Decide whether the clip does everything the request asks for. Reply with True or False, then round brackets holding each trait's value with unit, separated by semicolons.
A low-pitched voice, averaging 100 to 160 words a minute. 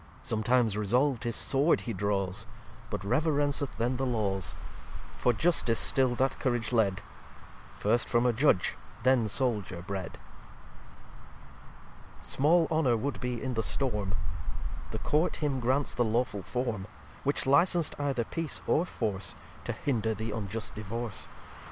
True (120 Hz; 140 wpm)